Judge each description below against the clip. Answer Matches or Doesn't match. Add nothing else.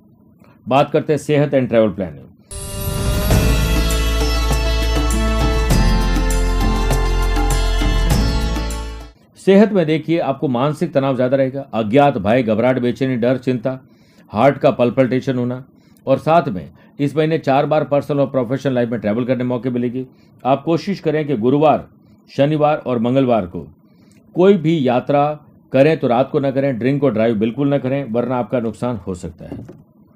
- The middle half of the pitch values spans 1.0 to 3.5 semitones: Doesn't match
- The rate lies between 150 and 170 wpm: Doesn't match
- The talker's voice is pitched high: Doesn't match